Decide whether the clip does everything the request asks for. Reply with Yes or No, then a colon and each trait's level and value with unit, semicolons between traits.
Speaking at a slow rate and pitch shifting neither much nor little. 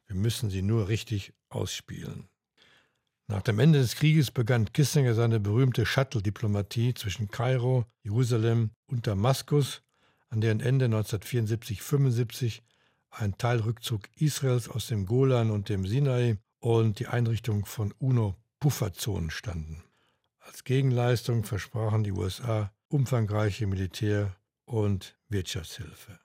Yes: slow, 110 wpm; average, 3.3 semitones